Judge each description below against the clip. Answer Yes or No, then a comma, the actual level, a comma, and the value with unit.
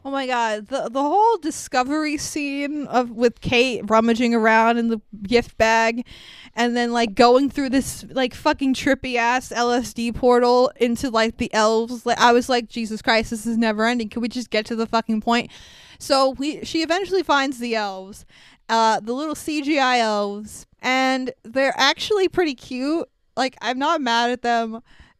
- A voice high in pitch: Yes, high, 240 Hz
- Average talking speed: Yes, average, 175 wpm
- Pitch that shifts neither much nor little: Yes, average, 3.0 semitones